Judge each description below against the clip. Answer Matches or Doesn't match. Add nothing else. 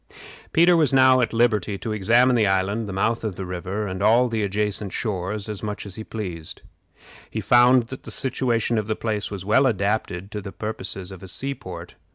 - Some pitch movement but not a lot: Matches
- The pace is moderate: Doesn't match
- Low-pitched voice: Matches